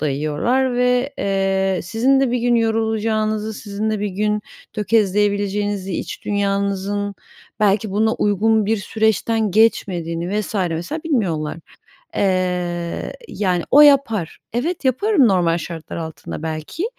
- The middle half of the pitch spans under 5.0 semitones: Yes, average, 3.4 semitones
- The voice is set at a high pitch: Yes, high, 205 Hz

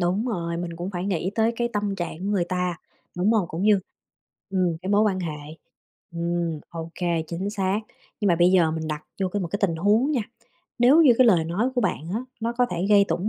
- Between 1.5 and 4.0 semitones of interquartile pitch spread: Yes, average, 3.5 semitones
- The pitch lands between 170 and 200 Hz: Yes, medium, 185 Hz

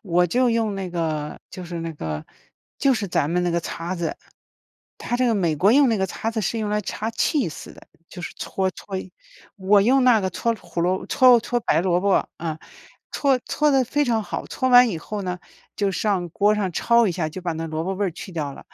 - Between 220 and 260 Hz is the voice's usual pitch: No, high, 190 Hz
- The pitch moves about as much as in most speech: Yes, average, 4.9 semitones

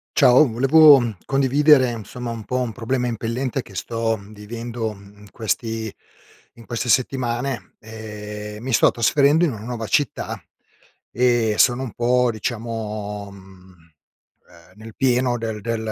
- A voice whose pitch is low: Yes, low, 115 Hz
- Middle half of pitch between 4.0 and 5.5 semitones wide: No, average, 2.8 semitones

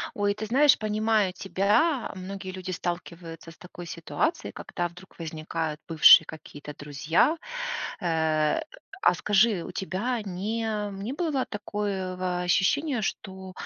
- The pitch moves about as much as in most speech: Yes, average, 4.1 semitones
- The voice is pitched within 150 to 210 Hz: Yes, medium, 185 Hz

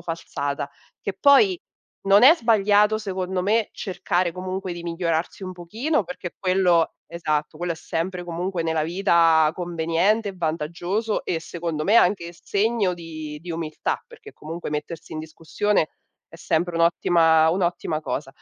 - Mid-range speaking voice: Yes, medium, 175 Hz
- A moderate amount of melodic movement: Yes, average, 3.1 semitones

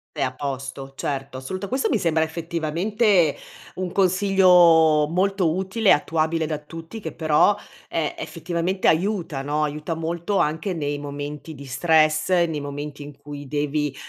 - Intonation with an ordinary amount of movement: Yes, average, 3.5 semitones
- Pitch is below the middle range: No, medium, 160 Hz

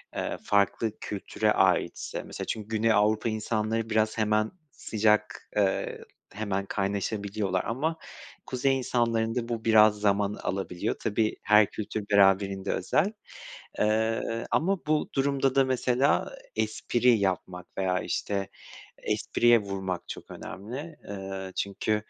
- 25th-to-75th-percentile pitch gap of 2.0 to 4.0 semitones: Yes, narrow, 2.6 semitones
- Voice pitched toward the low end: Yes, low, 110 Hz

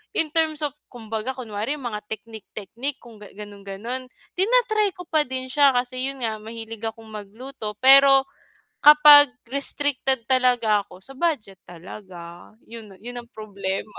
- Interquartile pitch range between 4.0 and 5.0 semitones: Yes, average, 4.5 semitones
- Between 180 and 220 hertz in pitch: No, high, 240 Hz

